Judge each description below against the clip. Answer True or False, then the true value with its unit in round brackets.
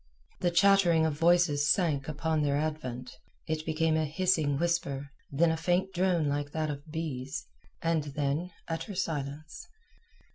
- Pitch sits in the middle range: True (155 Hz)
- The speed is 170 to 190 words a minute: False (145 wpm)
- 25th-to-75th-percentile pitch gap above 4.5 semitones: False (2.9 semitones)